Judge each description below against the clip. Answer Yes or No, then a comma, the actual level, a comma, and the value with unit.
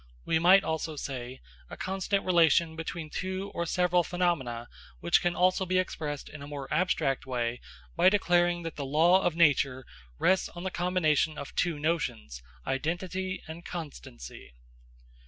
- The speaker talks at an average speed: Yes, average, 155 wpm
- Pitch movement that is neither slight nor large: Yes, average, 4.1 semitones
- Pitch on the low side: No, medium, 165 Hz